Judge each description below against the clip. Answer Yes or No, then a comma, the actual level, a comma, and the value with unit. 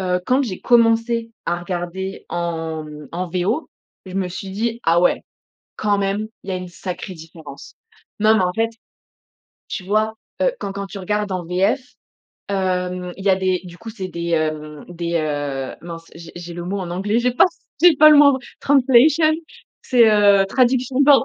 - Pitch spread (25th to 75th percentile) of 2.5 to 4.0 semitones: No, average, 4.6 semitones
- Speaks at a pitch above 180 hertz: Yes, high, 190 Hz